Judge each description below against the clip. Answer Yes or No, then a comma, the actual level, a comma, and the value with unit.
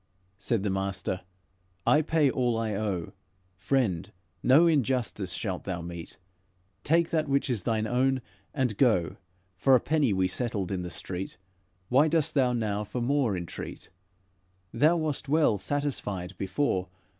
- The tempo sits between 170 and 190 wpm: No, average, 145 wpm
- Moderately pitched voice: No, low, 115 Hz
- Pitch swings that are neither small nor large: No, wide, 6.6 semitones